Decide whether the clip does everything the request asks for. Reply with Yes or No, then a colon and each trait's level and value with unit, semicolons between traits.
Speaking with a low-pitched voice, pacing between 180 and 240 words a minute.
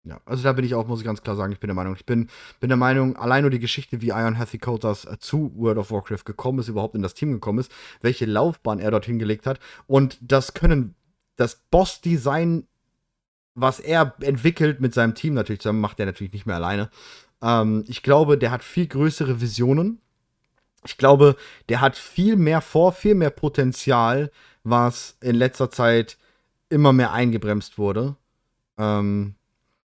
Yes: low, 125 Hz; average, 185 wpm